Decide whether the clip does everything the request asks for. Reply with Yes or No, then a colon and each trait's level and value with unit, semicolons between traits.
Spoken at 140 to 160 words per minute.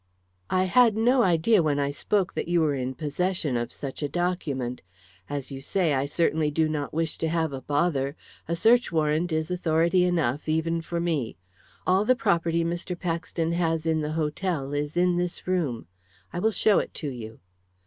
No: average, 190 wpm